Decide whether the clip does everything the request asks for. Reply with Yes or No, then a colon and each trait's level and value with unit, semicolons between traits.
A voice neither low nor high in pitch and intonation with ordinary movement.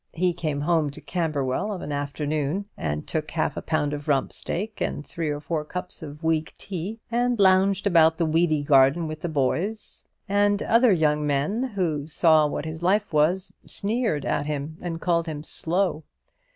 Yes: medium, 160 Hz; average, 4.0 semitones